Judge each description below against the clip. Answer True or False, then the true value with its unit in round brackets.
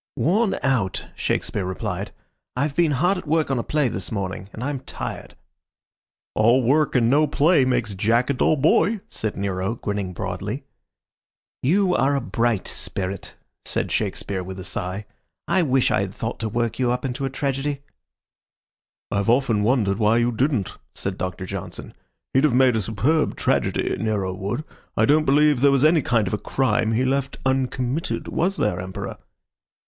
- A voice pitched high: False (125 Hz)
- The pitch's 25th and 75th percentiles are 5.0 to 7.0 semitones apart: True (5.4 semitones)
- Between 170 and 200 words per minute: True (175 wpm)